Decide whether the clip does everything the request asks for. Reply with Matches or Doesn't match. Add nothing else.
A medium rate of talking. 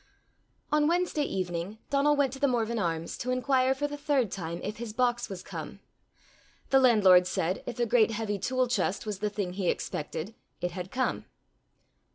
Matches